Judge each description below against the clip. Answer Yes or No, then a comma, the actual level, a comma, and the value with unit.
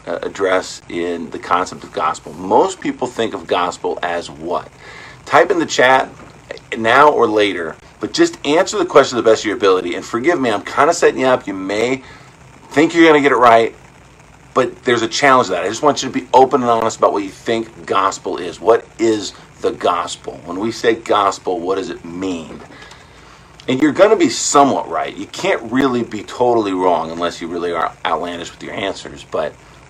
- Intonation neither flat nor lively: No, wide, 6.9 semitones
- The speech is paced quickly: Yes, fast, 210 wpm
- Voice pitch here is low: Yes, low, 115 Hz